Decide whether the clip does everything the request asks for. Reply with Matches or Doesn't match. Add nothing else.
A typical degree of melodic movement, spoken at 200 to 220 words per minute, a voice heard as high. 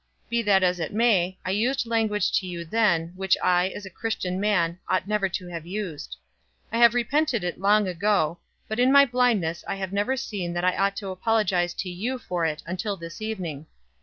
Matches